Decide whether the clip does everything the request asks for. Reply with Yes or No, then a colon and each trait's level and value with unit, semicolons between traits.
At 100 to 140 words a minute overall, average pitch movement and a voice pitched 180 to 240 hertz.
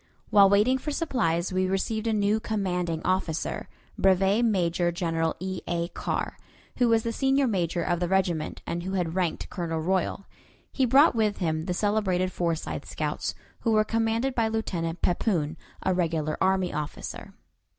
No: average, 160 wpm; average, 4.3 semitones; high, 190 Hz